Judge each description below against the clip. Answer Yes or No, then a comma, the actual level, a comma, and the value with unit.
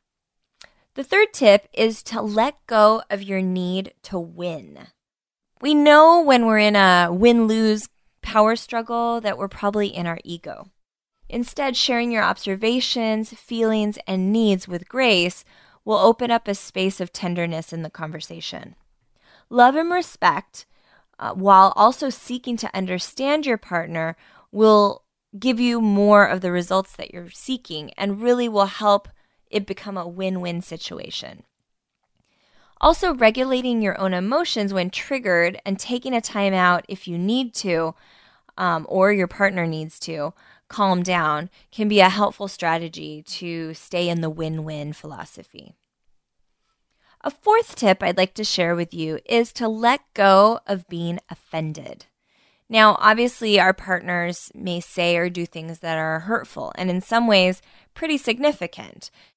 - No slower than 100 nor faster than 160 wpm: Yes, average, 150 wpm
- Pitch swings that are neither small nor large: Yes, average, 4.7 semitones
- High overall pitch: Yes, high, 200 Hz